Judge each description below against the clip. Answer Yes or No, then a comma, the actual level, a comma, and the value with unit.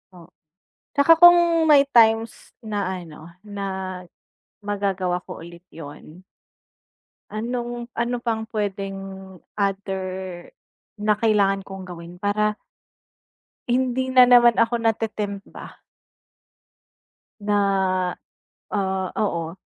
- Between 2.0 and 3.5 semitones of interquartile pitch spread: No, average, 3.9 semitones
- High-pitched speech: Yes, high, 205 Hz